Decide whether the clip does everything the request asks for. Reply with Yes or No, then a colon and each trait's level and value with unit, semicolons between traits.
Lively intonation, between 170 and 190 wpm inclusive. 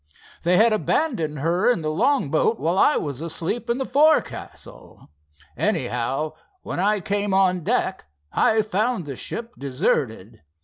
No: wide, 6.6 semitones; average, 145 wpm